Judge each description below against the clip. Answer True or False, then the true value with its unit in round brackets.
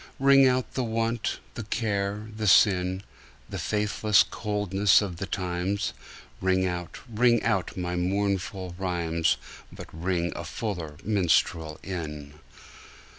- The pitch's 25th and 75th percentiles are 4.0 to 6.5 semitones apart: False (3.2 semitones)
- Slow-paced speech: True (125 wpm)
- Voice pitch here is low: True (95 Hz)